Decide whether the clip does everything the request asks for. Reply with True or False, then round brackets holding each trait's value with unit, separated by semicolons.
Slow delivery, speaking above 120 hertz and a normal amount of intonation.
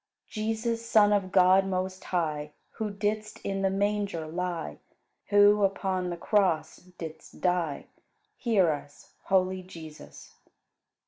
True (120 wpm; 190 Hz; 3.0 semitones)